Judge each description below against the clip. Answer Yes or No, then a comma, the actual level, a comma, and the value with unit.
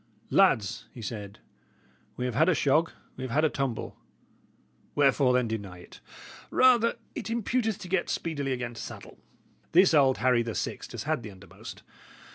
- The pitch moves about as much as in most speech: No, wide, 6.4 semitones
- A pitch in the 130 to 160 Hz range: Yes, low, 135 Hz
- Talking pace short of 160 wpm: No, average, 170 wpm